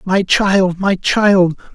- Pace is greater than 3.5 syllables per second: No, 2.7 syllables/s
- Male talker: Yes, male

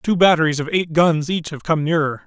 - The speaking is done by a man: Yes, male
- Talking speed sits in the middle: No, fast, 240 wpm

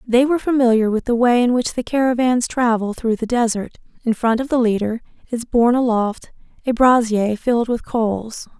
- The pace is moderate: Yes, average, 190 wpm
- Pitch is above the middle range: Yes, high, 235 Hz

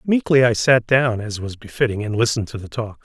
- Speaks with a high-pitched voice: No, low, 115 Hz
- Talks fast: Yes, fast, 235 wpm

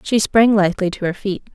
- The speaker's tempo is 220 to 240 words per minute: Yes, fast, 235 wpm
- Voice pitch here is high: Yes, high, 200 Hz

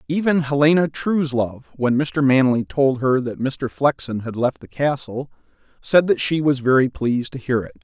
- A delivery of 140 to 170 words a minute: No, average, 185 wpm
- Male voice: Yes, male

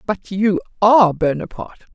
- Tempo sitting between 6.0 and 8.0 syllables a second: No, 5.6 syllables/s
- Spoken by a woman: Yes, female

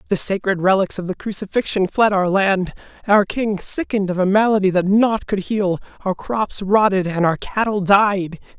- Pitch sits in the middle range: No, high, 195 Hz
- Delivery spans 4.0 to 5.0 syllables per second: Yes, 4.8 syllables/s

